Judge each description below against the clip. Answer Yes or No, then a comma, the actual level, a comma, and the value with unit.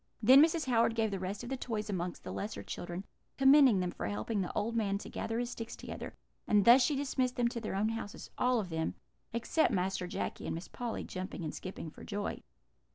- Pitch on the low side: No, high, 220 Hz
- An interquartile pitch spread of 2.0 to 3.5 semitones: No, average, 4.4 semitones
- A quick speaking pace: Yes, fast, 225 wpm